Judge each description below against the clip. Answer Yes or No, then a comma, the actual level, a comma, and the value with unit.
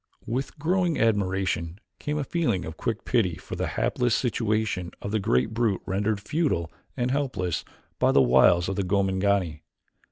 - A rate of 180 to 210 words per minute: No, average, 160 wpm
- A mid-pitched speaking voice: No, low, 100 Hz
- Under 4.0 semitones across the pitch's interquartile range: No, average, 5.1 semitones